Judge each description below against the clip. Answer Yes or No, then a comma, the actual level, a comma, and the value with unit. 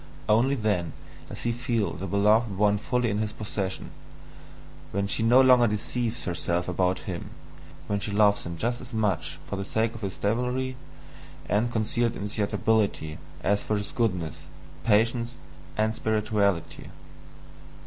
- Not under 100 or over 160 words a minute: Yes, average, 145 wpm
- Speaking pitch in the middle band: No, low, 105 Hz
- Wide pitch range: No, average, 2.8 semitones